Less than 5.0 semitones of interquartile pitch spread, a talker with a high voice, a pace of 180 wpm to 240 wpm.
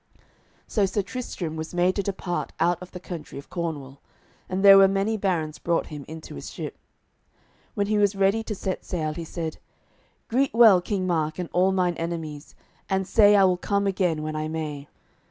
No: average, 3.6 semitones; medium, 180 Hz; average, 190 wpm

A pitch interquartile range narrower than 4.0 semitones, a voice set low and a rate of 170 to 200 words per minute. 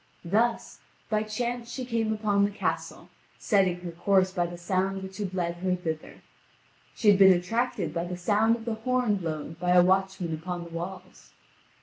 No: average, 3.4 semitones; high, 190 Hz; average, 185 wpm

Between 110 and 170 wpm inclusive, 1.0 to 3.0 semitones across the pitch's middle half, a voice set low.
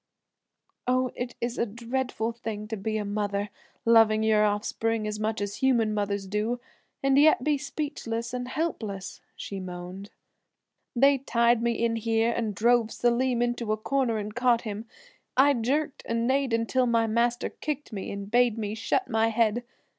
No: average, 165 wpm; narrow, 2.5 semitones; high, 230 Hz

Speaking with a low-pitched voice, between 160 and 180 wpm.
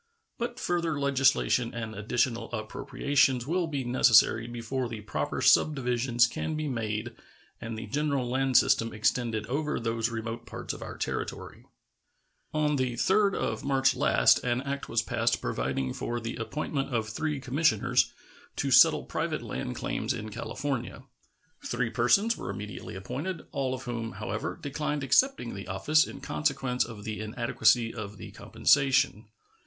No: low, 125 Hz; average, 150 wpm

